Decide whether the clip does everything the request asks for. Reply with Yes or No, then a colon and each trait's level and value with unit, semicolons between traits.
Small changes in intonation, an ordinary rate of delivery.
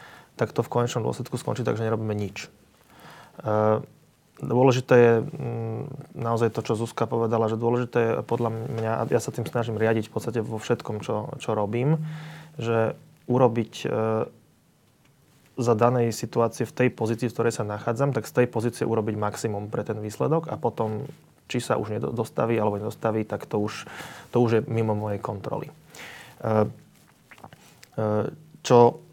Yes: narrow, 2.2 semitones; average, 150 wpm